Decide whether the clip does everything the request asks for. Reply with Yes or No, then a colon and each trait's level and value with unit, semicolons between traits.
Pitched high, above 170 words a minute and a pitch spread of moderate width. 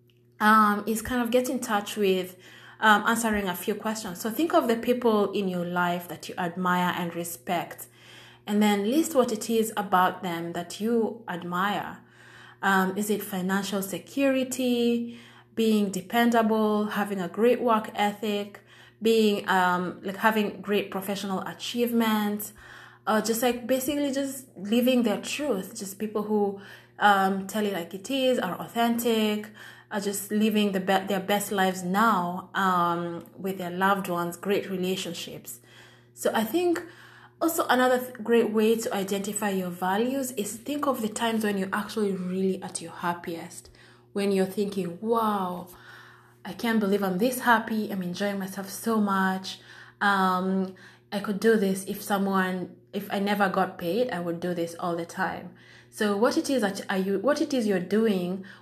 No: high, 205 Hz; average, 165 wpm; average, 3.4 semitones